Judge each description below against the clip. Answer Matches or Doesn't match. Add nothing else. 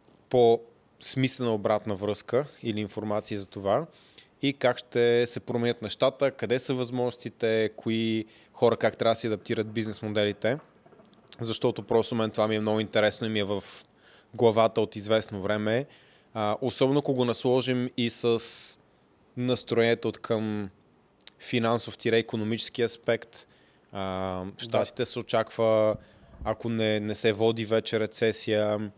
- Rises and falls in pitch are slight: Matches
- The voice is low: Matches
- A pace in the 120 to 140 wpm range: Matches